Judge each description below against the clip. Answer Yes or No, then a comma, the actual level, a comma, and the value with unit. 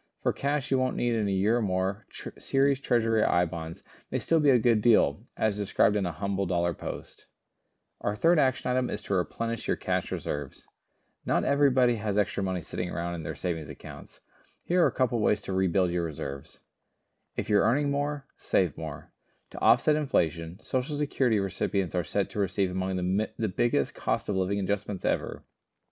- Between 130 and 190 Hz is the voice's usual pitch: No, low, 100 Hz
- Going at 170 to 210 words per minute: Yes, average, 195 wpm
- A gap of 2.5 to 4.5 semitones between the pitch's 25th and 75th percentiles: No, average, 5.3 semitones